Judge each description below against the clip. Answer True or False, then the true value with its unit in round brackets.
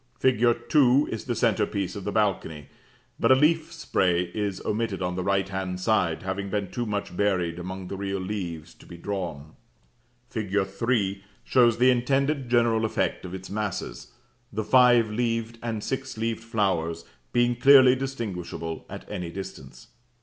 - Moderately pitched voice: False (105 Hz)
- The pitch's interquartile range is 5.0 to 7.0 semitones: False (4.3 semitones)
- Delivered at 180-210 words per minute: False (165 wpm)